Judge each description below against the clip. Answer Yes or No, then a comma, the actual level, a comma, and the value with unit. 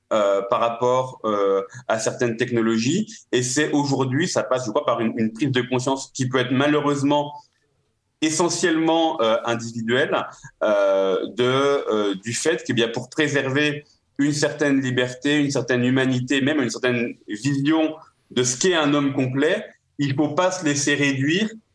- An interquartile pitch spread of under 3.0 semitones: No, average, 3.3 semitones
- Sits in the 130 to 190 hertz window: Yes, low, 135 Hz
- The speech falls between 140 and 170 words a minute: Yes, average, 160 wpm